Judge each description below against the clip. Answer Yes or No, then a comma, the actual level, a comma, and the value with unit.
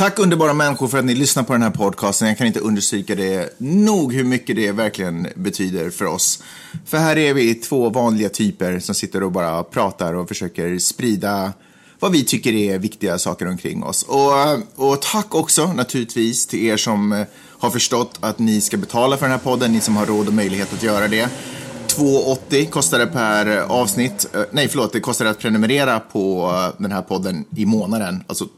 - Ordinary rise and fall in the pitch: Yes, average, 4.5 semitones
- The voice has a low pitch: Yes, low, 110 Hz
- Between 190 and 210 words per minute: Yes, fast, 195 wpm